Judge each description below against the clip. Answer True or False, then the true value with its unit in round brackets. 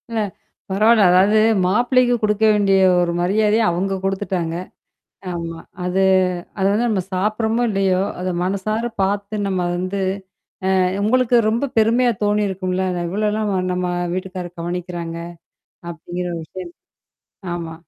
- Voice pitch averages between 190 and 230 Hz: True (195 Hz)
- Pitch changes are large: False (3.0 semitones)